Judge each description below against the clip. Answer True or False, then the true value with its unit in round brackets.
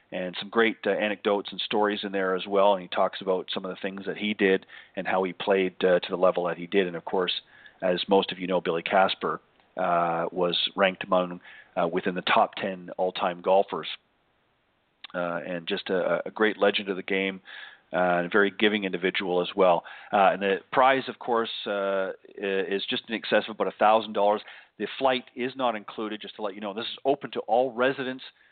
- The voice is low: True (100 Hz)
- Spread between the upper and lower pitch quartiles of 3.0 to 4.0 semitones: True (3.4 semitones)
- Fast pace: True (215 wpm)